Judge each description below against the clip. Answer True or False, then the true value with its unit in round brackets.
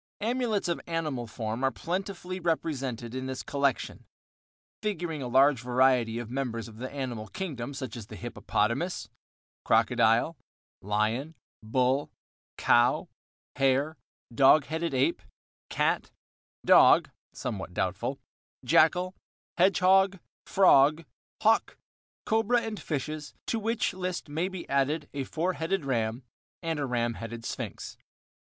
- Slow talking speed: True (120 wpm)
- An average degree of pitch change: False (5.9 semitones)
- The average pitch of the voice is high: False (140 Hz)